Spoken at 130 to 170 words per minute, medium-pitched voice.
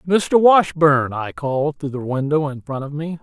No: fast, 205 wpm; medium, 150 Hz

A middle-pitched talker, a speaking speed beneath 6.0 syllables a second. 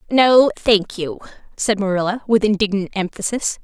No: high, 215 Hz; 4.8 syllables/s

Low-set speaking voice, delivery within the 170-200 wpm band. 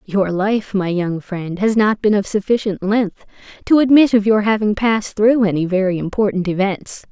No: high, 205 Hz; average, 185 wpm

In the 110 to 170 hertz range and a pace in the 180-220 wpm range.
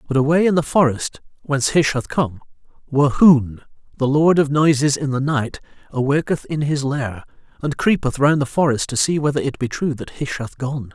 Yes: medium, 140 Hz; average, 195 wpm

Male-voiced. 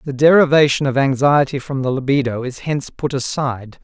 Yes: male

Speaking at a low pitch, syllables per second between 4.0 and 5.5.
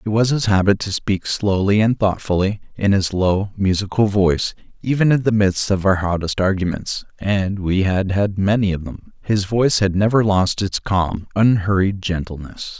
Yes: low, 100 Hz; 4.7 syllables/s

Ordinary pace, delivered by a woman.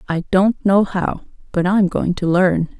Yes: average, 170 wpm; female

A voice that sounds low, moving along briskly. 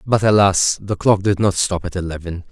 Yes: very low, 95 Hz; fast, 215 wpm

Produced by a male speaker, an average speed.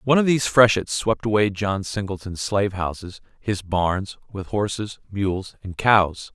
Yes: male; average, 160 wpm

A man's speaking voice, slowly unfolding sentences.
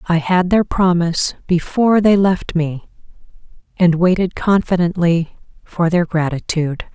No: female; slow, 120 wpm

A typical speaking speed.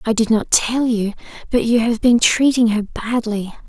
Yes: average, 195 wpm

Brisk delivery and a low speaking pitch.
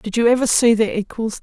No: fast, 250 wpm; high, 225 Hz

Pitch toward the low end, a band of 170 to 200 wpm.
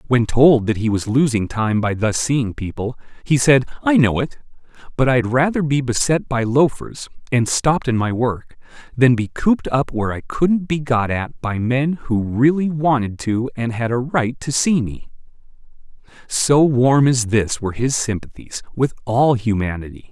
Yes: low, 125 Hz; average, 180 wpm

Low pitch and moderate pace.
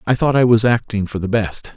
No: low, 115 Hz; fast, 275 wpm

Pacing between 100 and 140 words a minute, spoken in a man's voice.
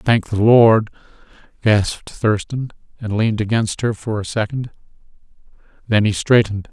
Yes: slow, 135 wpm; male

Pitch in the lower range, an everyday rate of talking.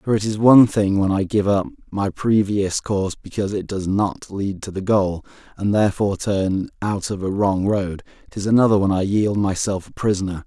No: low, 100 Hz; fast, 210 wpm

